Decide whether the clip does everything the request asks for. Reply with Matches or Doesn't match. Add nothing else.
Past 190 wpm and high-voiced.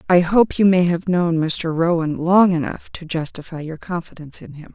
Doesn't match